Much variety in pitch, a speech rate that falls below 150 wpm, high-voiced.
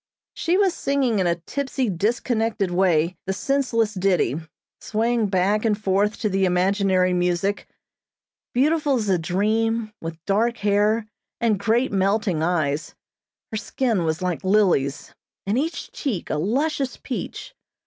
No: average, 4.2 semitones; average, 140 wpm; high, 205 Hz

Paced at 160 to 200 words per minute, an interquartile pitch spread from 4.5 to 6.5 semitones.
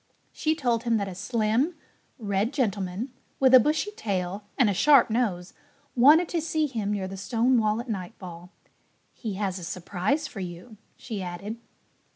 Yes: average, 170 wpm; average, 5.2 semitones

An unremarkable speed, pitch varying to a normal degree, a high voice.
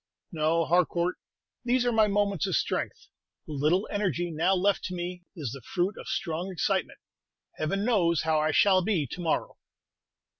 No: average, 165 wpm; average, 3.7 semitones; medium, 175 Hz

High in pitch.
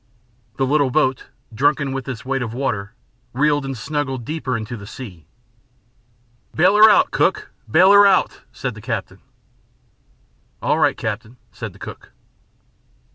No: low, 135 Hz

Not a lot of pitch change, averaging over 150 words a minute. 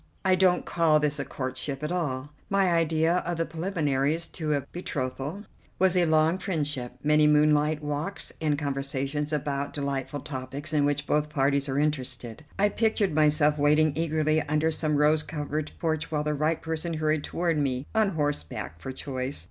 Yes: narrow, 2.2 semitones; average, 170 wpm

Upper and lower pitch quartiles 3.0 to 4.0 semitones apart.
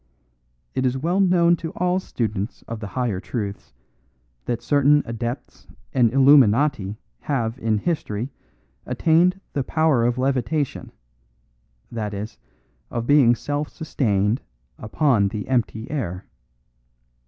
No: average, 5.2 semitones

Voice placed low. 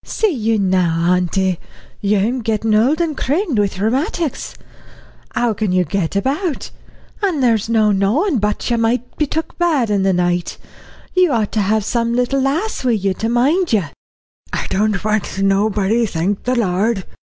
No: high, 220 Hz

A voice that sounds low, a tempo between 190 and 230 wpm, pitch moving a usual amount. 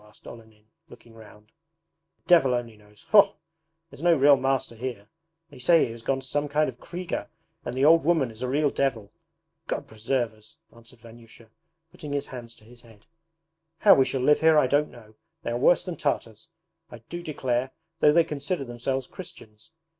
Yes: low, 130 Hz; average, 195 wpm; average, 4.5 semitones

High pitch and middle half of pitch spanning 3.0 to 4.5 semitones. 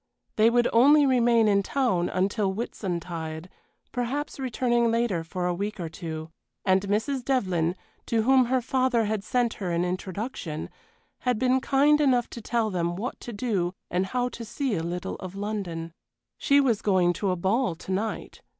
No: high, 215 Hz; wide, 5.5 semitones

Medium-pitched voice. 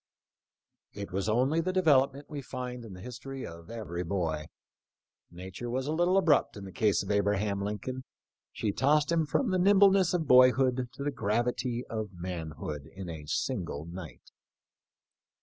No: low, 120 Hz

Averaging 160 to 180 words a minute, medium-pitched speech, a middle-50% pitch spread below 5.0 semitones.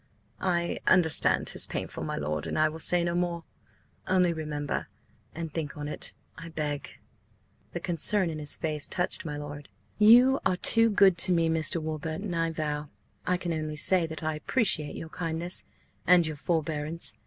Yes: average, 165 wpm; medium, 165 Hz; narrow, 2.5 semitones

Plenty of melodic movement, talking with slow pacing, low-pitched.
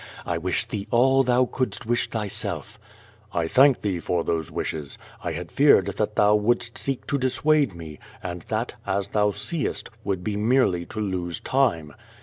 No: wide, 6.3 semitones; average, 170 wpm; low, 105 Hz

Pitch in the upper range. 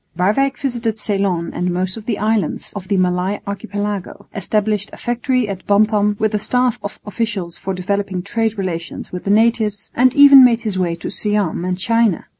Yes: high, 205 Hz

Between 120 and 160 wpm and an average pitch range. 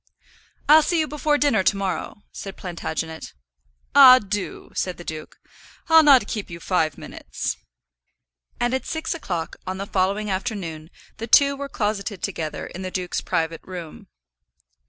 No: average, 155 wpm; wide, 6.7 semitones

